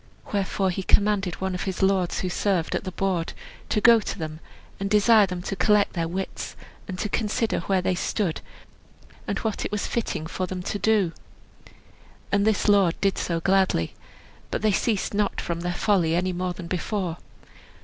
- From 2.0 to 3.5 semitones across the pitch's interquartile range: Yes, narrow, 2.5 semitones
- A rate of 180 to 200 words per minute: Yes, average, 185 wpm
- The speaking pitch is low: No, high, 190 Hz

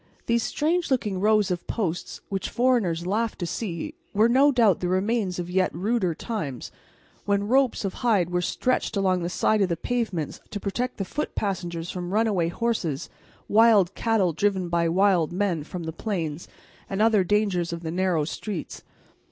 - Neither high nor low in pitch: No, high, 195 Hz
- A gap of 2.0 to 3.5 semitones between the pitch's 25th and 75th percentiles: No, average, 4.2 semitones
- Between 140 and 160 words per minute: No, average, 175 wpm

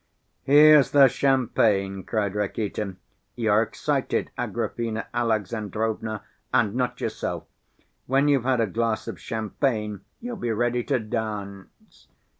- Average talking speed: No, slow, 115 wpm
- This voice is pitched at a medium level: No, low, 115 Hz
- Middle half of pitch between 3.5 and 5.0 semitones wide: No, average, 3.1 semitones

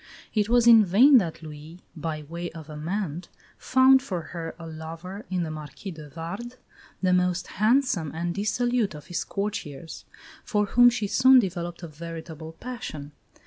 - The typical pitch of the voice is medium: Yes, medium, 175 Hz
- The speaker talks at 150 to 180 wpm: Yes, average, 160 wpm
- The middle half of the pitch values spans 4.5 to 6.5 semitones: Yes, average, 5.1 semitones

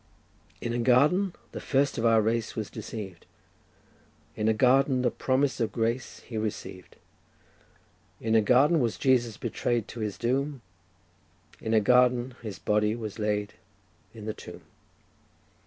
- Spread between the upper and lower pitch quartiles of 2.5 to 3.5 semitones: Yes, average, 2.9 semitones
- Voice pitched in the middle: No, low, 115 Hz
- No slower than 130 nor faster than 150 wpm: Yes, average, 145 wpm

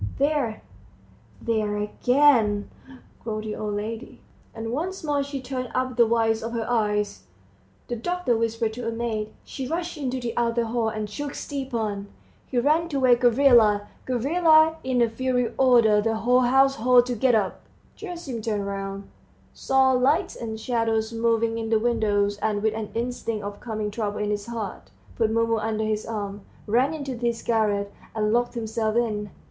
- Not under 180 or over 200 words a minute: No, average, 170 wpm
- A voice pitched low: No, high, 230 Hz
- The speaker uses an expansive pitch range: No, average, 2.9 semitones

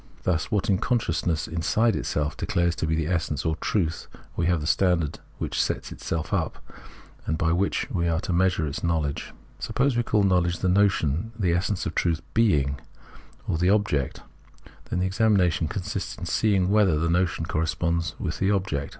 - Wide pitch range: No, average, 3.3 semitones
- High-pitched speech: No, very low, 85 Hz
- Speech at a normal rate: Yes, average, 185 wpm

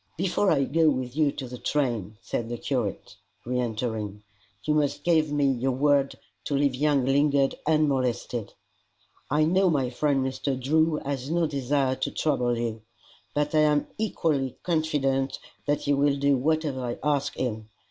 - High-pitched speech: No, medium, 140 Hz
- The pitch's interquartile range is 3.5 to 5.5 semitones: No, average, 3.0 semitones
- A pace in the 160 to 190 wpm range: Yes, average, 165 wpm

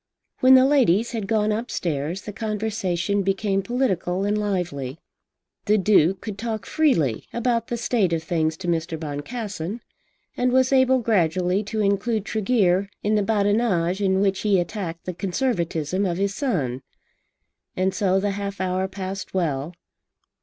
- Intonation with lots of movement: No, average, 3.7 semitones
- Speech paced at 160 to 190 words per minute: No, average, 150 wpm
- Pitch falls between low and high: No, high, 195 Hz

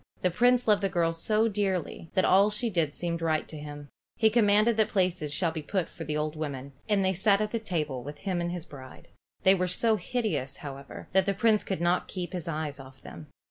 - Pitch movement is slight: No, average, 5.1 semitones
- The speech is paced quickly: Yes, fast, 230 wpm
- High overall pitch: No, medium, 180 Hz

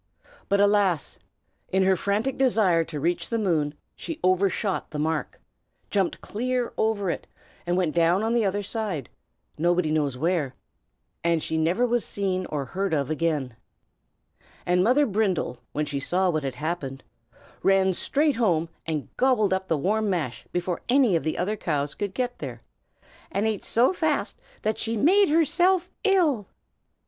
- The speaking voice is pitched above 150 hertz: Yes, high, 190 Hz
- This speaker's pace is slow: No, average, 160 wpm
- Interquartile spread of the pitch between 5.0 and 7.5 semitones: Yes, wide, 5.6 semitones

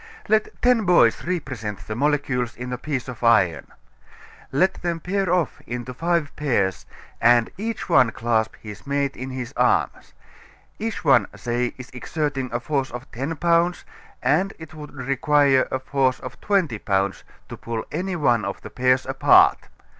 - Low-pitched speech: Yes, low, 130 Hz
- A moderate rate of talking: Yes, average, 160 wpm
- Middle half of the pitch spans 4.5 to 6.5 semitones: Yes, average, 5.3 semitones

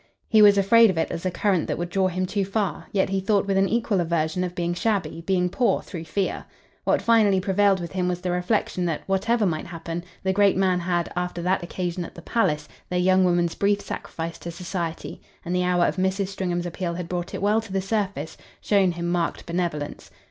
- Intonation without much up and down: Yes, narrow, 2.2 semitones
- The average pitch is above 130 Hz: Yes, medium, 185 Hz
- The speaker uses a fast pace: Yes, fast, 220 wpm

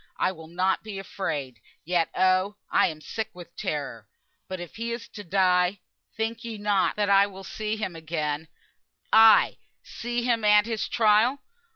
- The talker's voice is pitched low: No, high, 195 Hz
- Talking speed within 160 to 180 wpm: Yes, average, 175 wpm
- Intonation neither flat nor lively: Yes, average, 4.0 semitones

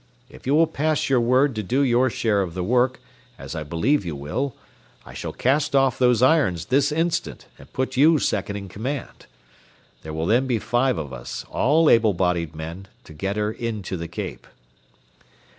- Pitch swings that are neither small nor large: No, wide, 6.8 semitones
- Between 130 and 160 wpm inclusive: No, average, 195 wpm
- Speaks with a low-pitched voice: Yes, low, 120 Hz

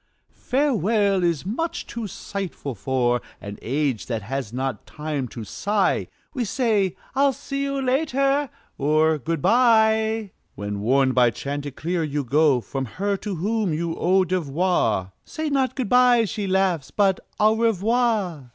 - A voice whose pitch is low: No, medium, 185 Hz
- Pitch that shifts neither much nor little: No, wide, 8.4 semitones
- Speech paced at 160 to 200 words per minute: No, average, 145 wpm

